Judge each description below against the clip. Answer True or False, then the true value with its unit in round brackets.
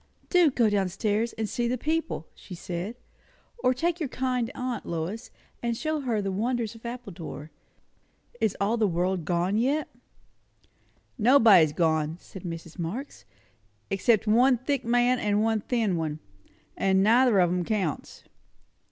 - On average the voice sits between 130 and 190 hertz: False (220 Hz)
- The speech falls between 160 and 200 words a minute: False (150 wpm)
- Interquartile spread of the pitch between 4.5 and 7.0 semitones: True (5.4 semitones)